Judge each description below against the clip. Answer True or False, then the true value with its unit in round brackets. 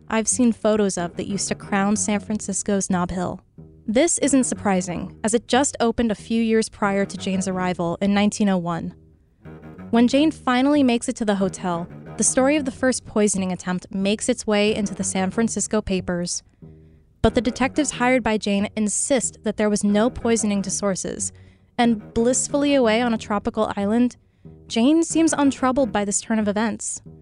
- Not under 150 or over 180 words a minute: True (175 wpm)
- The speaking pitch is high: True (210 Hz)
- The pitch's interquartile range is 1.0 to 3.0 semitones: False (4.2 semitones)